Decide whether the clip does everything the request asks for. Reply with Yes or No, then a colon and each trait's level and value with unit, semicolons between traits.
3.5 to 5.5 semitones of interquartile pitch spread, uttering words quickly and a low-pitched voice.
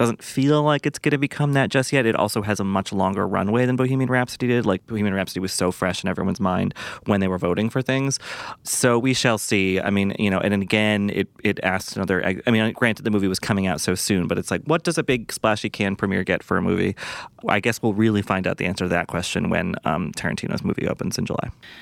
Yes: average, 4.6 semitones; fast, 255 wpm; low, 105 Hz